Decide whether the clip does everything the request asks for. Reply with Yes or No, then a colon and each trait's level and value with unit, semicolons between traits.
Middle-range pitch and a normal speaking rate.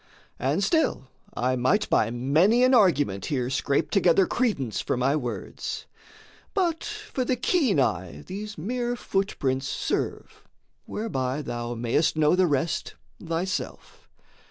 No: medium, 160 Hz; slow, 130 wpm